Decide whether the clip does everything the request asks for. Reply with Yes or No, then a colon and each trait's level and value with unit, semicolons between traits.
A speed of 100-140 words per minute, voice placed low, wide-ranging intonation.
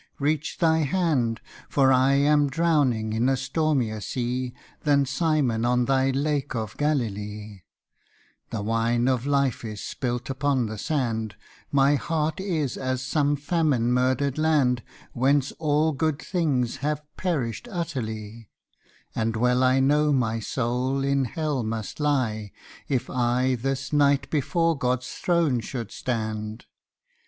No: slow, 135 wpm; low, 130 Hz; average, 3.7 semitones